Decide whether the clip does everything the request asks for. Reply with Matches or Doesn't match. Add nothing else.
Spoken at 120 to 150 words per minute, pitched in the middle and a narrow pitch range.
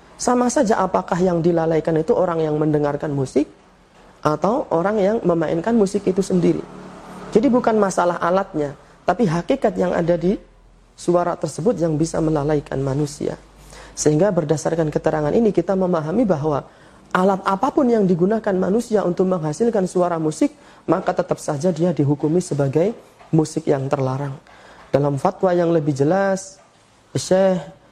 Doesn't match